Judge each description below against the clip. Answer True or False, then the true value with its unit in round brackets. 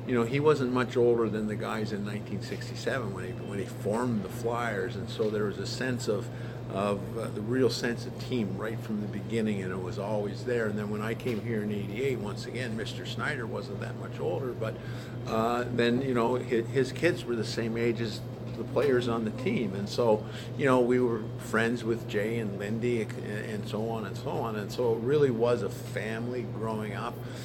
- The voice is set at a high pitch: False (115 Hz)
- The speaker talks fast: True (220 wpm)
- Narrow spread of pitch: True (1.8 semitones)